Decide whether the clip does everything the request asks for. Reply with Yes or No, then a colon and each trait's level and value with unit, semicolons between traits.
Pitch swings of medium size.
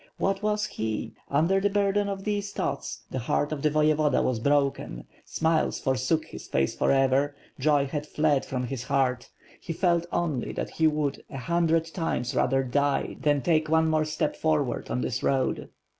Yes: average, 3.6 semitones